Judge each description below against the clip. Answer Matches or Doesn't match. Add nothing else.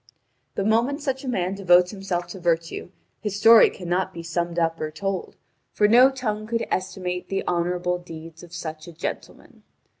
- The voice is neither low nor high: Matches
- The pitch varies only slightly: Doesn't match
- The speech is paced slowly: Doesn't match